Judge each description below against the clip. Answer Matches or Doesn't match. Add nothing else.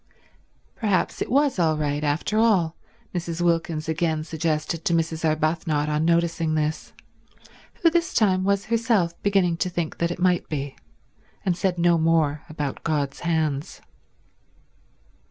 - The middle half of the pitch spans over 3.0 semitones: Doesn't match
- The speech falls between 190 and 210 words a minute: Doesn't match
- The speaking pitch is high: Doesn't match